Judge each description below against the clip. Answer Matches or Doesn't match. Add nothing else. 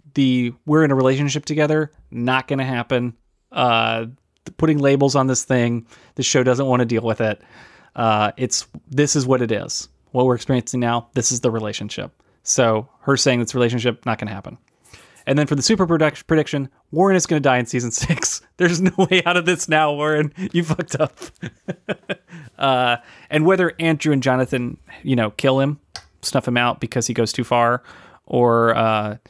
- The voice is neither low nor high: Doesn't match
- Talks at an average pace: Matches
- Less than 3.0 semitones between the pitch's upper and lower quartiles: Doesn't match